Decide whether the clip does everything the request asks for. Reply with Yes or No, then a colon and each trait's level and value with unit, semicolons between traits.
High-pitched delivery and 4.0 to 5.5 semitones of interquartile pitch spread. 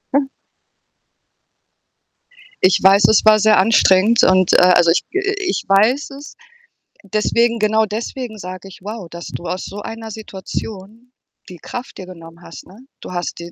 No: high, 205 Hz; average, 3.5 semitones